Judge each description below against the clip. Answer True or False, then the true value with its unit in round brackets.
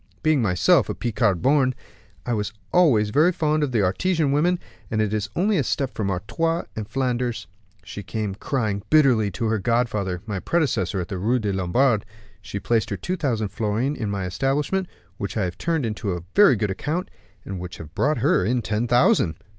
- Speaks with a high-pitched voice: False (115 Hz)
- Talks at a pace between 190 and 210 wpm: True (195 wpm)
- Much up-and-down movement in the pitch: True (5.9 semitones)